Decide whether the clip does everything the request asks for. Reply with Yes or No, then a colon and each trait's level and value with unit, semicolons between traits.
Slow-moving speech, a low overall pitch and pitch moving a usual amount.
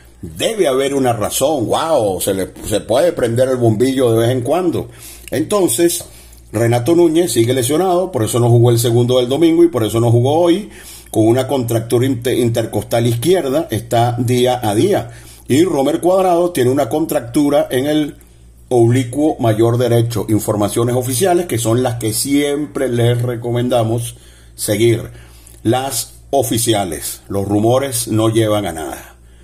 No: average, 150 wpm; low, 120 Hz; average, 3.5 semitones